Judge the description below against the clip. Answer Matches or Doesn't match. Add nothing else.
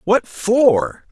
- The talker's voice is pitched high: Matches